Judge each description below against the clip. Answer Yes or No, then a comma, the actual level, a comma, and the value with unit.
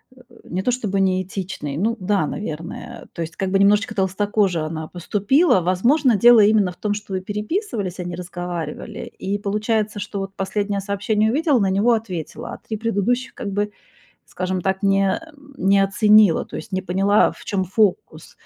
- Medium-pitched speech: No, high, 200 Hz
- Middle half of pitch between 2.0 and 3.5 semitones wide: Yes, narrow, 2.4 semitones